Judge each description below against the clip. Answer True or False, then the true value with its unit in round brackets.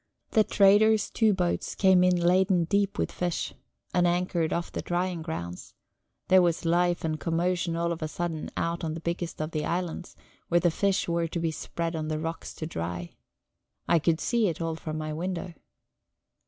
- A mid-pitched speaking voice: True (170 Hz)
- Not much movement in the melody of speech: True (1.9 semitones)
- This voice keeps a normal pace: True (190 wpm)